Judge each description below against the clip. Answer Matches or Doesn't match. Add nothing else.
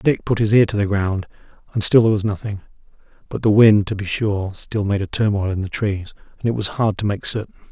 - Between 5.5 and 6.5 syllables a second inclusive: Matches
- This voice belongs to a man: Matches